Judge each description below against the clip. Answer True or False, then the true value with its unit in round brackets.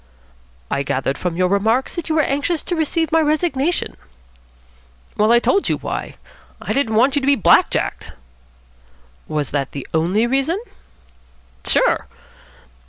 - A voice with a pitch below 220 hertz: False (265 Hz)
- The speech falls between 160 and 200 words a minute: False (145 wpm)